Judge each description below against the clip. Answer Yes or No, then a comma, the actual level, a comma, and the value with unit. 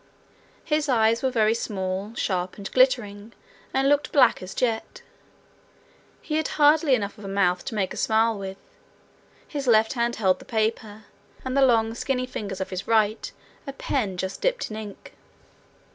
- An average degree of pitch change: Yes, average, 4.3 semitones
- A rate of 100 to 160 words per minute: No, average, 170 wpm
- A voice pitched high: Yes, high, 225 Hz